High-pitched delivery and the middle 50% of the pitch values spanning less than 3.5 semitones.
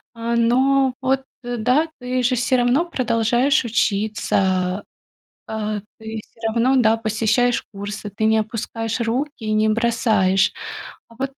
Yes: high, 230 Hz; narrow, 2.5 semitones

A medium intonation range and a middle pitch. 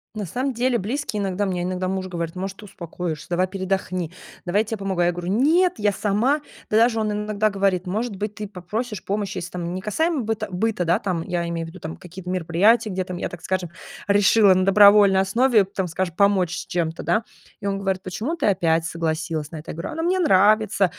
No: average, 3.0 semitones; high, 195 Hz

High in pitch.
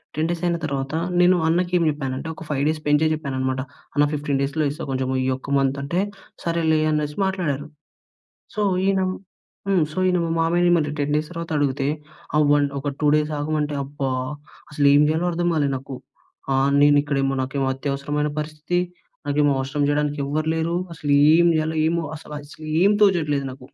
No: medium, 150 Hz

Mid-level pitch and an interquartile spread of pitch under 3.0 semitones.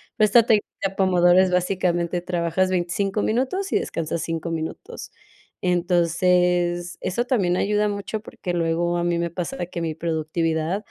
Yes: medium, 180 Hz; narrow, 2.4 semitones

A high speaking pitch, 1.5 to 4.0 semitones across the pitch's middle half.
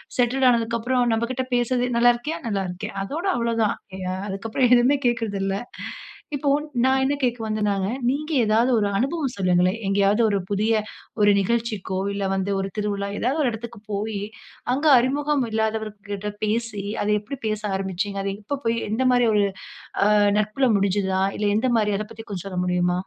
Yes: high, 220 Hz; average, 3.5 semitones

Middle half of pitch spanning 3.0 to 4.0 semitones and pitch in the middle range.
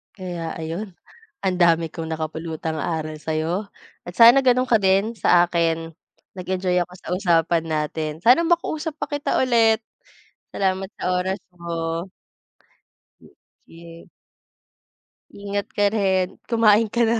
No: average, 4.6 semitones; medium, 180 Hz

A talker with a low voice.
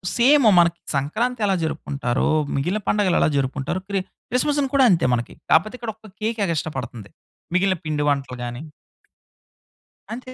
No: medium, 185 Hz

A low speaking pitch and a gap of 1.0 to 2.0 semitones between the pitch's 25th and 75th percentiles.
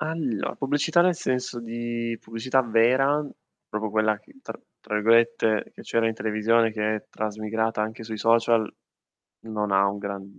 Yes: low, 115 Hz; narrow, 1.7 semitones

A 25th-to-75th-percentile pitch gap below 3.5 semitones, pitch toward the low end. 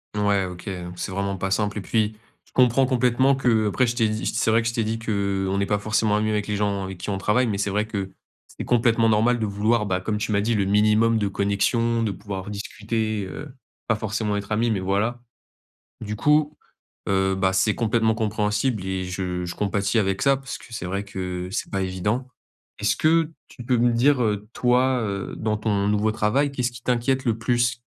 Yes: average, 2.9 semitones; low, 105 Hz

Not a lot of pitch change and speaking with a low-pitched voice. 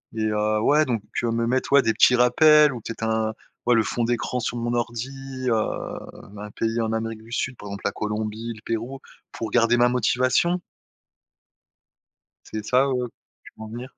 Yes: narrow, 2.3 semitones; low, 115 Hz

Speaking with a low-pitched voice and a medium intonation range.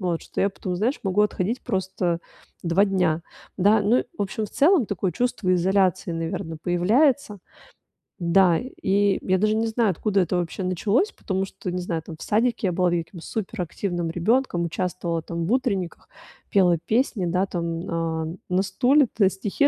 No: high, 190 Hz; average, 3.4 semitones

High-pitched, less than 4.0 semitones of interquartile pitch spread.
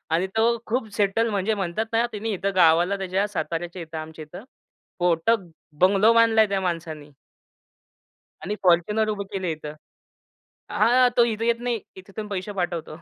No: high, 195 Hz; average, 4.3 semitones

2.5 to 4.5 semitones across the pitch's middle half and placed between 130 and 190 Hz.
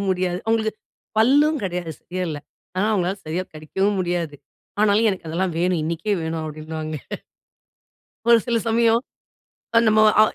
No: average, 5.0 semitones; medium, 185 Hz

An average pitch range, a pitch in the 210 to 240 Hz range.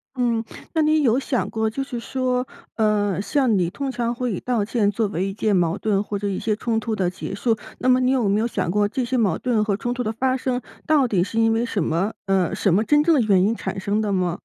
Yes: average, 3.8 semitones; high, 220 Hz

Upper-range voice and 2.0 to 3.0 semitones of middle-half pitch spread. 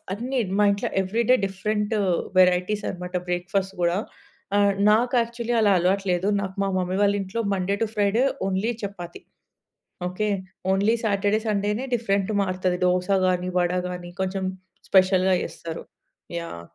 Yes: high, 195 Hz; narrow, 2.4 semitones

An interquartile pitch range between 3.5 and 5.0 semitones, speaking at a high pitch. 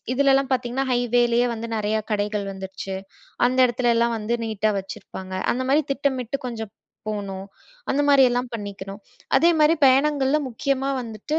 Yes: average, 4.1 semitones; high, 240 Hz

